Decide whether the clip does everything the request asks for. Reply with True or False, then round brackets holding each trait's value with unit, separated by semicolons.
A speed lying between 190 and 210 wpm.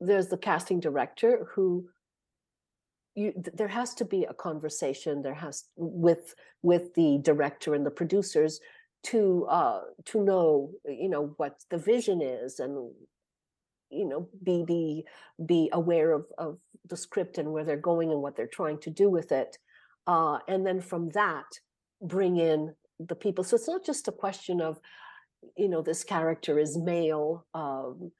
False (165 wpm)